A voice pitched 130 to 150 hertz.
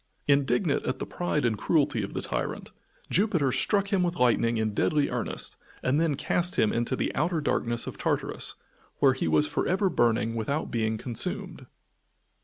Yes: low, 135 Hz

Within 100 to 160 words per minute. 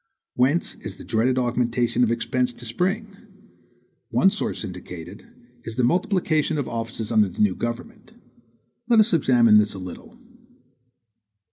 Yes: average, 140 wpm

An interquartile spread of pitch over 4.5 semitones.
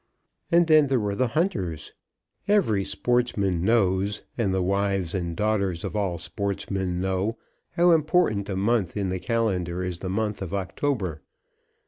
No: average, 4.0 semitones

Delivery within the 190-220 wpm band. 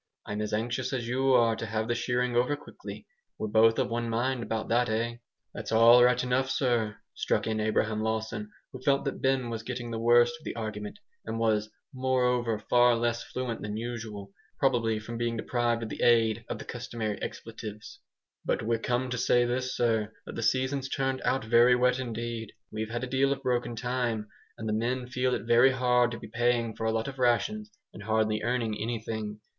Yes: fast, 205 wpm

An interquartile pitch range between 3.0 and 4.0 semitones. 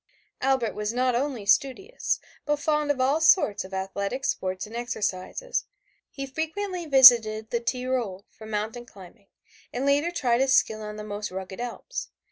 No: average, 4.7 semitones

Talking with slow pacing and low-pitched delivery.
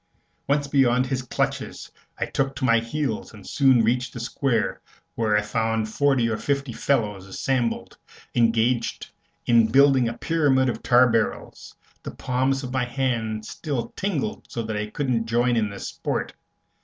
No: average, 160 wpm; low, 120 Hz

